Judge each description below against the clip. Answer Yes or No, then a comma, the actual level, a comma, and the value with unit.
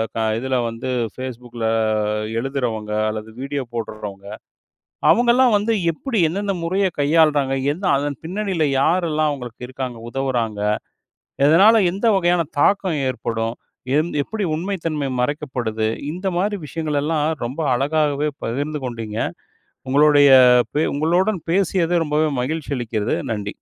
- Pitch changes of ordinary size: No, wide, 5.7 semitones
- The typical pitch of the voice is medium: Yes, medium, 145 Hz